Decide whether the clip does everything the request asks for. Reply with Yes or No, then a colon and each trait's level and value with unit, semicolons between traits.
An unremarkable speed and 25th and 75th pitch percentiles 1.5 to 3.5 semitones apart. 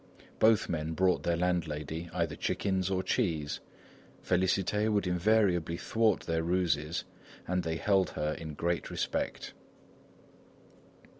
No: slow, 120 wpm; average, 2.7 semitones